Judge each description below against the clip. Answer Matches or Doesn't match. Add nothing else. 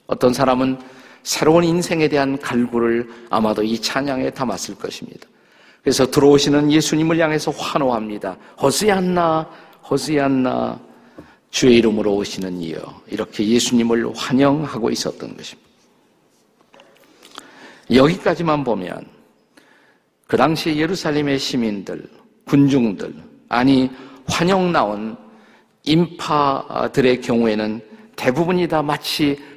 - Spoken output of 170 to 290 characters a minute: Matches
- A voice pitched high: Doesn't match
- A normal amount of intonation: Matches